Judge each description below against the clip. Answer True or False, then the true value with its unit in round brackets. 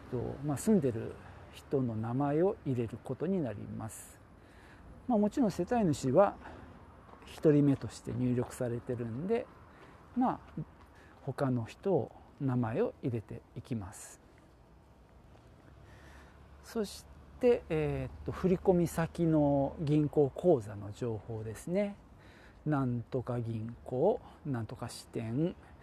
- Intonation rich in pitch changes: True (6.0 semitones)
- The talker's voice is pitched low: True (125 Hz)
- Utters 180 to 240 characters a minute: True (215 characters per minute)